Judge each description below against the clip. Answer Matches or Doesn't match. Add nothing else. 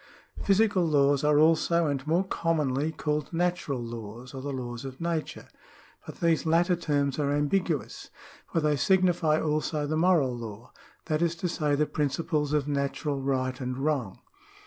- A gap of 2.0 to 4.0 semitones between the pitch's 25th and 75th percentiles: Matches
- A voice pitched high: Doesn't match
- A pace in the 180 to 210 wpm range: Doesn't match